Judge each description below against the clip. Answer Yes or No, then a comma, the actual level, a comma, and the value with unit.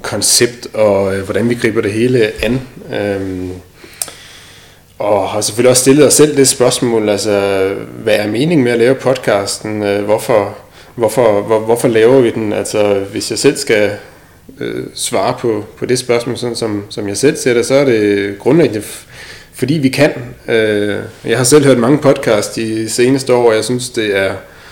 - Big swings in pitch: No, average, 3.6 semitones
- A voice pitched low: Yes, low, 115 Hz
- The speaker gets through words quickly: No, average, 180 wpm